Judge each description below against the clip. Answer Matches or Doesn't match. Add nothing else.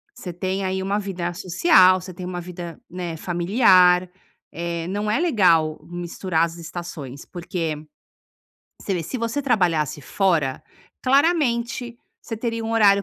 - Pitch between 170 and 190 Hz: Matches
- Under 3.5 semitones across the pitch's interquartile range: Doesn't match